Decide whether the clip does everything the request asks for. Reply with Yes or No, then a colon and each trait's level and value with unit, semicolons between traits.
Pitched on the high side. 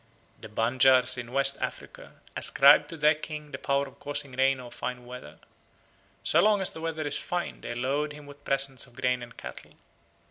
No: low, 135 Hz